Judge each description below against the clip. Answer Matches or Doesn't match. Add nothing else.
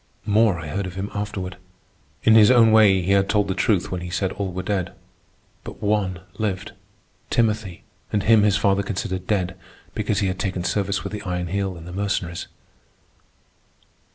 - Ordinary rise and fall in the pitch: Doesn't match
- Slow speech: Doesn't match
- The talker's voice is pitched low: Matches